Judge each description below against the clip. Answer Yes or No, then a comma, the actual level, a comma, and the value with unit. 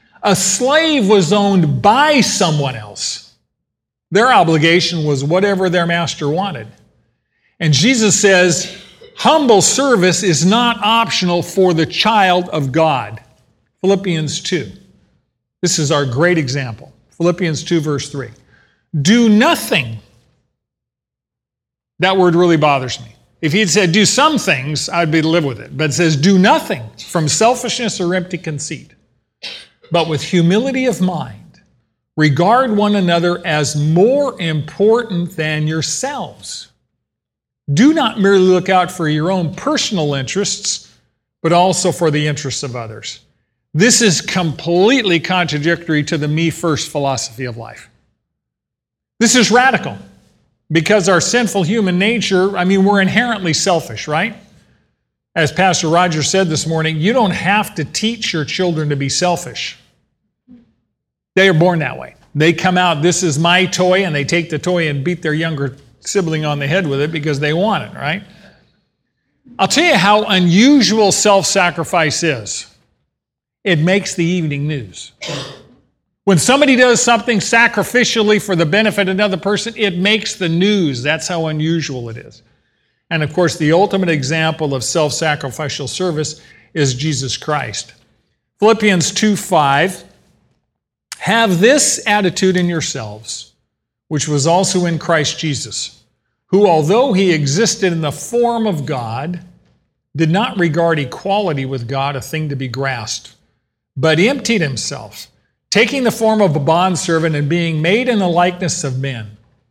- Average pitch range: Yes, average, 5.0 semitones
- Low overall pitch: No, medium, 170 Hz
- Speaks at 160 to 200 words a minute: No, average, 145 wpm